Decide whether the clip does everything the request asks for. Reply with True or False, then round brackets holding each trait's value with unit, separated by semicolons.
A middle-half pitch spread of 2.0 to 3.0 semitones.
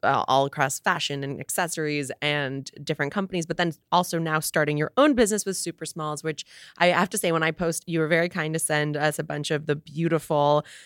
True (2.6 semitones)